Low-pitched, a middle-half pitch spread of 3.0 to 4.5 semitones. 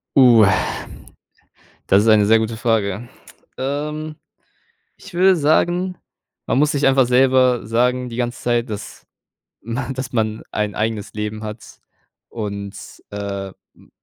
Yes: low, 120 Hz; average, 3.8 semitones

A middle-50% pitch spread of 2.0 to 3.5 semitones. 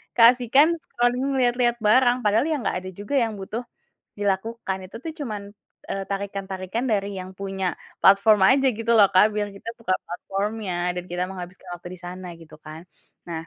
No: average, 4.1 semitones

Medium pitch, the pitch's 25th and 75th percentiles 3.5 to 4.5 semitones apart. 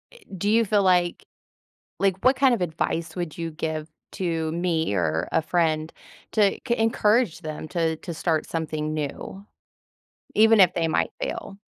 Yes: medium, 170 Hz; average, 3.8 semitones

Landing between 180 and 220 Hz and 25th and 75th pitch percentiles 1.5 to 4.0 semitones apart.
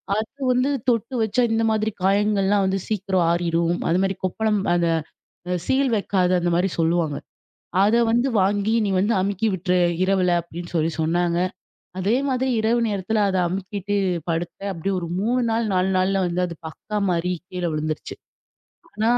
Yes: high, 190 Hz; average, 3.5 semitones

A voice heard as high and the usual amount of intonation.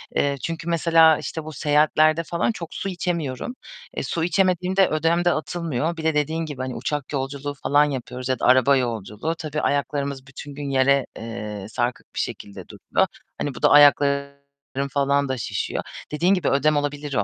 No: medium, 145 Hz; average, 3.3 semitones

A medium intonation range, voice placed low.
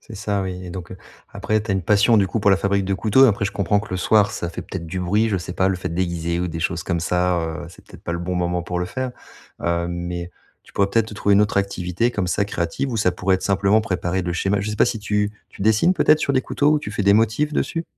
Yes: average, 3.1 semitones; very low, 95 Hz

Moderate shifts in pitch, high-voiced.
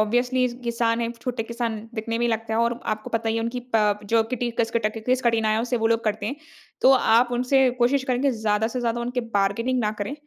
No: narrow, 1.9 semitones; high, 230 Hz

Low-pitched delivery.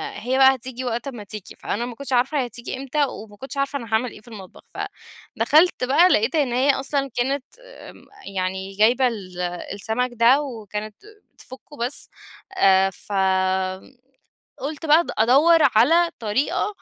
No: high, 245 Hz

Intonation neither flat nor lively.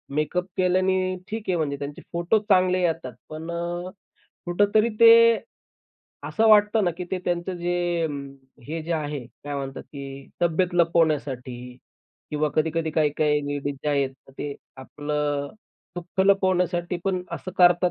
Yes: average, 3.9 semitones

